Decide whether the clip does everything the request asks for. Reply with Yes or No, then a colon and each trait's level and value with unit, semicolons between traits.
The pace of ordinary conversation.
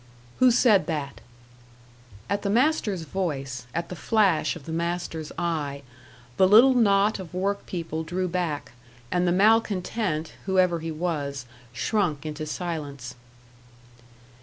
No: slow, 130 wpm